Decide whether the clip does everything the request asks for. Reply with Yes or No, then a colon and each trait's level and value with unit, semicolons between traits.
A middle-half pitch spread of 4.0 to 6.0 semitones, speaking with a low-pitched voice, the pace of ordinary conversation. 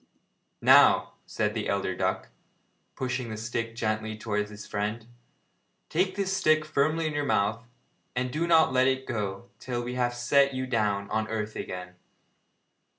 Yes: average, 4.3 semitones; low, 120 Hz; average, 155 wpm